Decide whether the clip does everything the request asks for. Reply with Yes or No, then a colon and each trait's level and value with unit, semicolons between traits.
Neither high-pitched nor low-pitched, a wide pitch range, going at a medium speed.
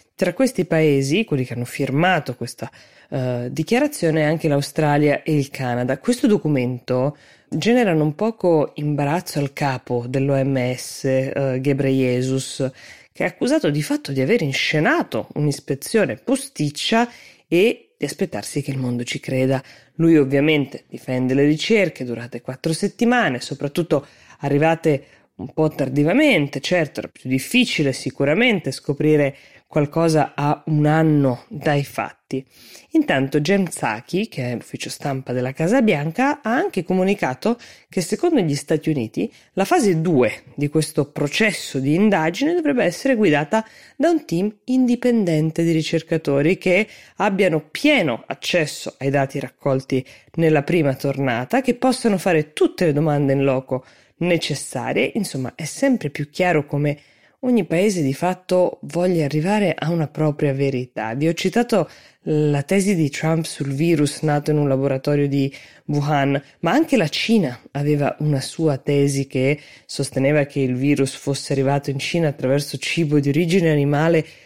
No: medium, 150 Hz; average, 4.4 semitones; average, 140 wpm